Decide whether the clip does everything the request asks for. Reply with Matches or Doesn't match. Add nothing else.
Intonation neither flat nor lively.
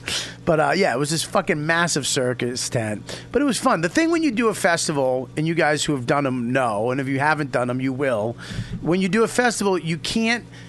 Doesn't match